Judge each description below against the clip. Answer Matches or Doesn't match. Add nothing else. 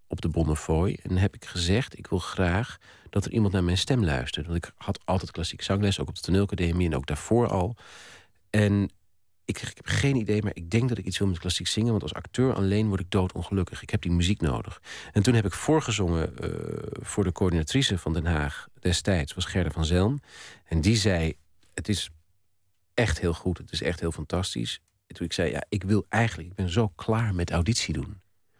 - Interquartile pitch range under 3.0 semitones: Doesn't match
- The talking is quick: Matches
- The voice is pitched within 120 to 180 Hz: Doesn't match